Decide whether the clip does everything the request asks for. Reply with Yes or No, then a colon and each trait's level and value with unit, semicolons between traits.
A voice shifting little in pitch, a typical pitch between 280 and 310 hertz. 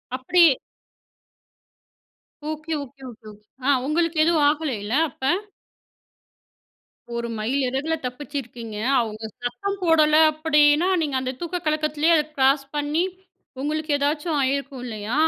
No: average, 3.4 semitones; very high, 290 Hz